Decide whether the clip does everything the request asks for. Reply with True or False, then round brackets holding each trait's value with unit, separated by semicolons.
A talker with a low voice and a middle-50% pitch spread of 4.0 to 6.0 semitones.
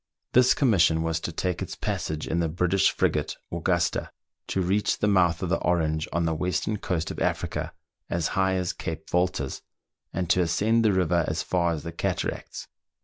False (85 Hz; 2.4 semitones)